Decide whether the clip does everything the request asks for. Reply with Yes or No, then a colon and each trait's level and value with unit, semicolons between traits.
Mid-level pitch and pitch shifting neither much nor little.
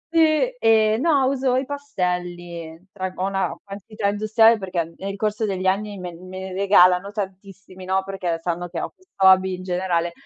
No: high, 195 Hz; average, 3.0 semitones